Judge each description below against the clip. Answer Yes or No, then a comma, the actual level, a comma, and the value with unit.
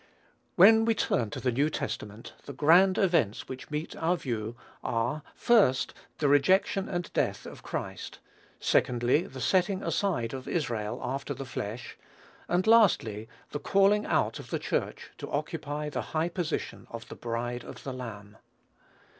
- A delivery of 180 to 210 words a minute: No, average, 155 wpm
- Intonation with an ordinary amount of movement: No, wide, 7.1 semitones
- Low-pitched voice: No, medium, 145 Hz